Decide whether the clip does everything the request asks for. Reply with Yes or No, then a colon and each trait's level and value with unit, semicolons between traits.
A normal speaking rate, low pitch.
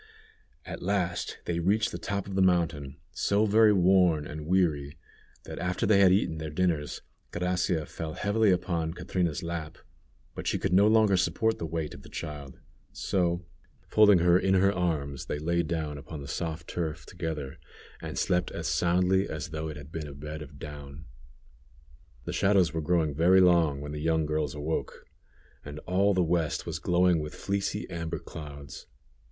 Yes: average, 175 wpm; very low, 85 Hz